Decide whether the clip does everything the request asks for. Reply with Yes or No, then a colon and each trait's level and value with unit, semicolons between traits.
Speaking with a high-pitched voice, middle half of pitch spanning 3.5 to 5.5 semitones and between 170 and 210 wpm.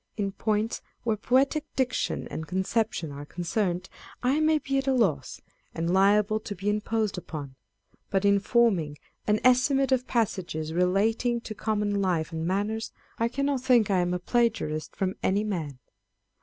No: high, 205 Hz; average, 4.9 semitones; average, 160 wpm